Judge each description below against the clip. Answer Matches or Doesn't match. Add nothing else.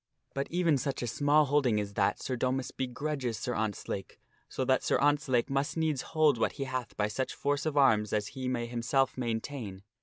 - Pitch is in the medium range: Doesn't match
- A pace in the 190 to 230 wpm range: Matches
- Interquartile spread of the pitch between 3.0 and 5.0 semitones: Matches